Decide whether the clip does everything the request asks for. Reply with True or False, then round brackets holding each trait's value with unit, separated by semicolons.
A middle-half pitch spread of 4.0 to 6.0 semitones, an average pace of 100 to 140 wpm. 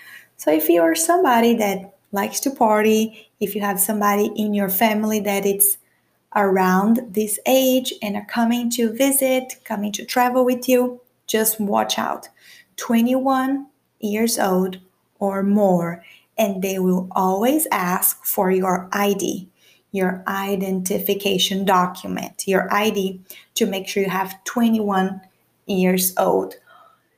False (3.2 semitones; 130 wpm)